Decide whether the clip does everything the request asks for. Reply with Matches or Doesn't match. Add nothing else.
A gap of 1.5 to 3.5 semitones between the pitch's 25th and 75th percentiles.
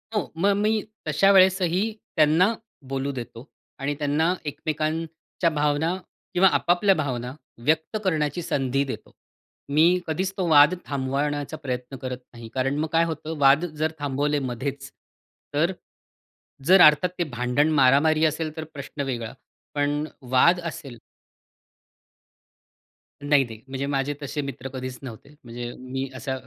Matches